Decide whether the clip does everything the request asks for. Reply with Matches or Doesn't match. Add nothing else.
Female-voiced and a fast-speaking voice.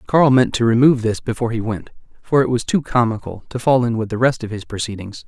Doesn't match